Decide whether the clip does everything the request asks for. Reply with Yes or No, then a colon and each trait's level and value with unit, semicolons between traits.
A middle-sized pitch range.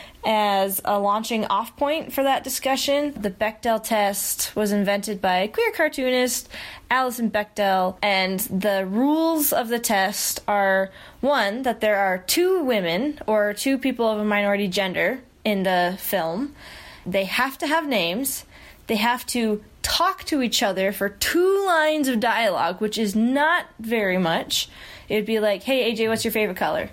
Yes: average, 4.9 semitones